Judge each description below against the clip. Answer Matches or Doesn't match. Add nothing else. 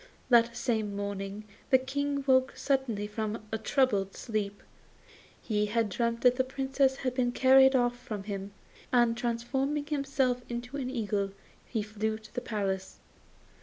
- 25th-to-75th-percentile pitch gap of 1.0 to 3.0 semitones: Doesn't match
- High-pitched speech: Matches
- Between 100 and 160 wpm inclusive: Matches